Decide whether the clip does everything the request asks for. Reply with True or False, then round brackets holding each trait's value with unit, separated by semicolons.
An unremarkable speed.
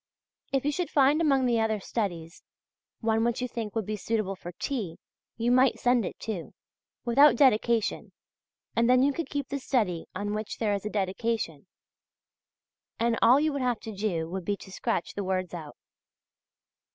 True (180 wpm)